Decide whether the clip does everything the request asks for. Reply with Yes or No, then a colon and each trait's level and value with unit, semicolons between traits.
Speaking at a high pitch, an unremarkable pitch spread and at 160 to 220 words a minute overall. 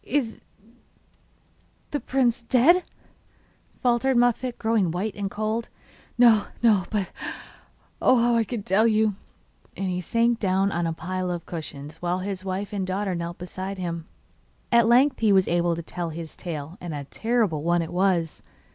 Yes: high, 195 Hz; average, 4.9 semitones; average, 165 wpm